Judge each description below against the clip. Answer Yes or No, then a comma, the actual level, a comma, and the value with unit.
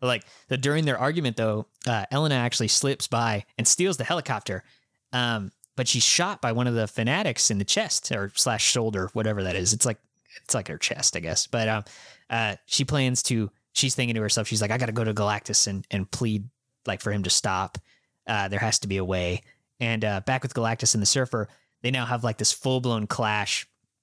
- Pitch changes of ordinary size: Yes, average, 3.4 semitones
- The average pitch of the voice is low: Yes, low, 115 Hz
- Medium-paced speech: No, fast, 225 wpm